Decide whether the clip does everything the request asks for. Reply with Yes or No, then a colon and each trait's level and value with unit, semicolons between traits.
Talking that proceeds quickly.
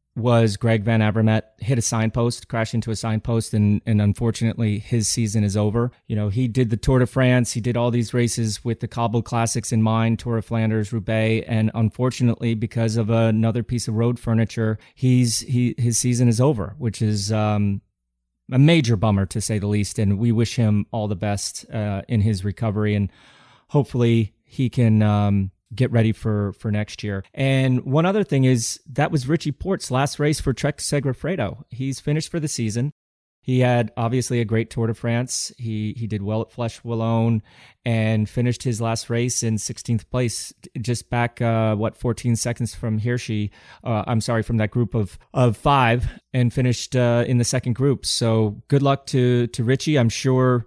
No: average, 190 wpm